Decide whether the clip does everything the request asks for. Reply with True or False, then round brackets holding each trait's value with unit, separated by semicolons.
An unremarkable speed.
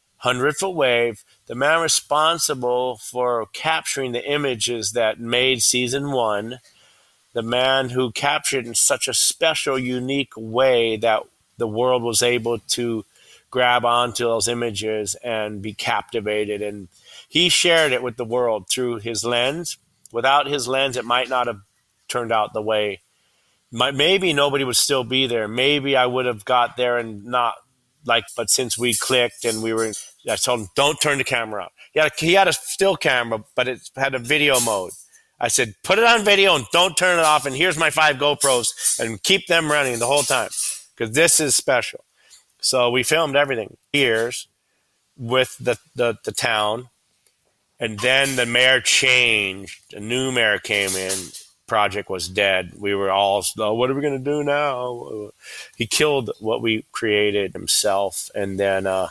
True (175 wpm)